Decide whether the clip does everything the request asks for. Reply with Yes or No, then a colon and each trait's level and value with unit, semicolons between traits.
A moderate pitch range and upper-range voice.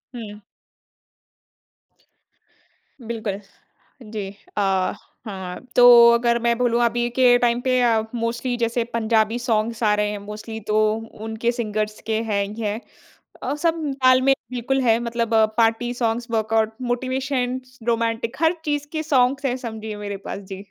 No: narrow, 2.2 semitones; high, 235 Hz